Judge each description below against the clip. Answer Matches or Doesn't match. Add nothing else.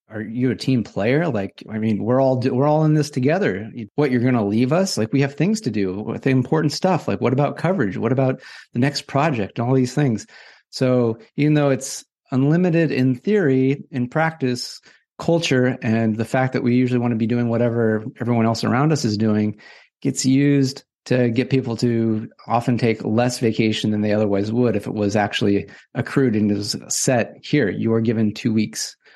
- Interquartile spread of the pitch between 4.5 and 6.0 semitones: Doesn't match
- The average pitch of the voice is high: Doesn't match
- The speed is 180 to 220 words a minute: Matches